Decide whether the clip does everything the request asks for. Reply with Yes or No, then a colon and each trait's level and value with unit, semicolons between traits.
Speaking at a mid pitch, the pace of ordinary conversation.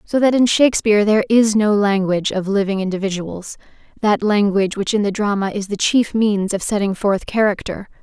No: high, 205 Hz; average, 180 wpm